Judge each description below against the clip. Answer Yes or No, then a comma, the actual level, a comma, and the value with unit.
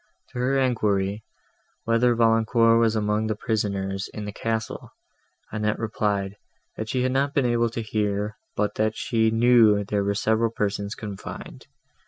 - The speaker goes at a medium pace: Yes, average, 155 wpm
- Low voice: Yes, low, 110 Hz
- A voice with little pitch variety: Yes, narrow, 2.0 semitones